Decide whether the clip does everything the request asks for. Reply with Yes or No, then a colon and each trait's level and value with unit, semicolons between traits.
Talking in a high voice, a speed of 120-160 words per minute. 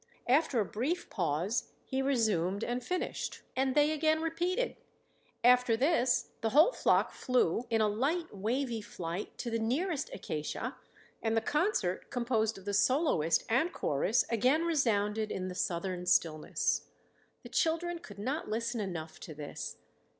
Yes: high, 235 Hz; average, 150 wpm